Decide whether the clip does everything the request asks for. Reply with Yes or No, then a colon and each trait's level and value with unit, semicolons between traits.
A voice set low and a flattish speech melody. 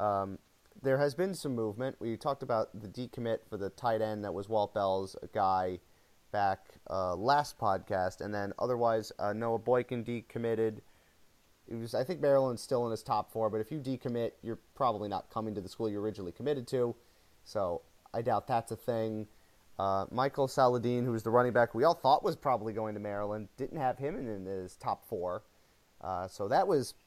No: low, 110 Hz; average, 3.4 semitones